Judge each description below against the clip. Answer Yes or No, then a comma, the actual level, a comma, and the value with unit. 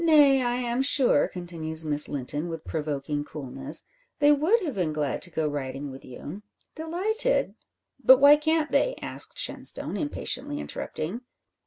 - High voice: Yes, high, 200 Hz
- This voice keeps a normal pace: Yes, average, 155 wpm